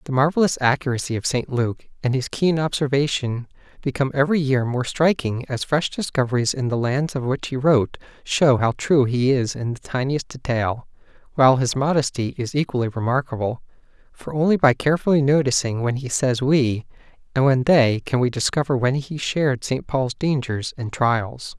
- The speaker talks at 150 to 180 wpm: Yes, average, 175 wpm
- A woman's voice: No, male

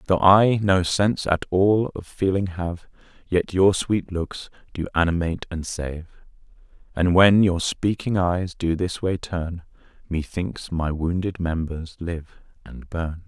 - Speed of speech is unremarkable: Yes, average, 150 wpm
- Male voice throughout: Yes, male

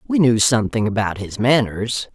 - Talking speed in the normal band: Yes, average, 170 wpm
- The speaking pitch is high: No, low, 115 Hz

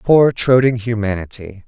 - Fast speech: No, slow, 105 wpm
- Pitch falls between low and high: No, low, 115 Hz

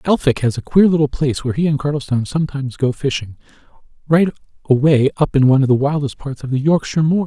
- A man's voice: Yes, male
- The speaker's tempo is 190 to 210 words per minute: Yes, fast, 205 wpm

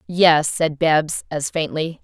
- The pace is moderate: Yes, average, 150 wpm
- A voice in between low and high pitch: Yes, medium, 155 Hz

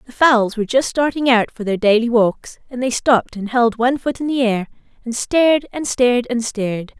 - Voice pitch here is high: Yes, high, 240 Hz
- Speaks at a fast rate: Yes, fast, 225 wpm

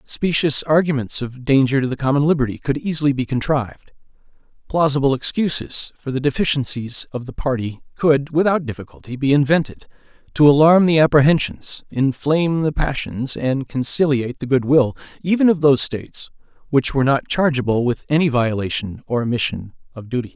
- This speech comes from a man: Yes, male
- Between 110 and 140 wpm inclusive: No, average, 155 wpm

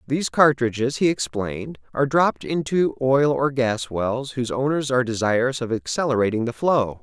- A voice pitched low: Yes, low, 130 Hz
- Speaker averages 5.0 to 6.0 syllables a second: Yes, 5.4 syllables/s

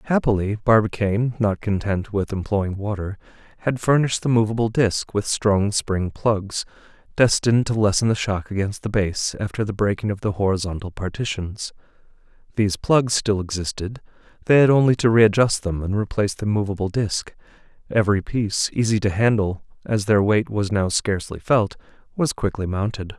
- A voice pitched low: Yes, low, 105 Hz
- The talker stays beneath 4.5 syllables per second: No, 5.3 syllables/s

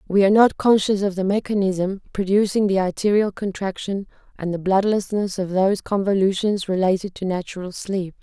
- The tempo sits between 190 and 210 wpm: No, average, 155 wpm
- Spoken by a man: No, female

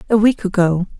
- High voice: Yes, high, 200 Hz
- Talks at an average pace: Yes, average, 180 wpm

